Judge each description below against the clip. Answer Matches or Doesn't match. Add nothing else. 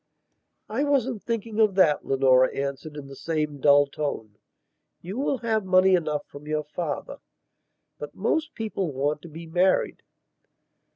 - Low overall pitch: Doesn't match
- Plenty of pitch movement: Matches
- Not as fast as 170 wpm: Matches